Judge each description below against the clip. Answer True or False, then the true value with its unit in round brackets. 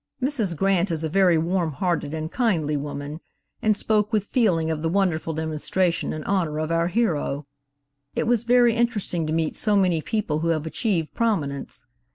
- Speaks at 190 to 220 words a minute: False (180 wpm)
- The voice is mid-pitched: True (170 Hz)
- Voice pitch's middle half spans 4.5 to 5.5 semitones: True (4.9 semitones)